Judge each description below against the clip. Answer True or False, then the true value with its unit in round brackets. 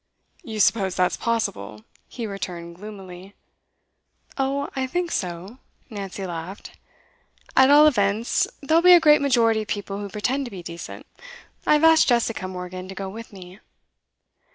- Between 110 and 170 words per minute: True (155 wpm)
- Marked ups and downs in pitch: True (6.0 semitones)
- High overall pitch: True (205 Hz)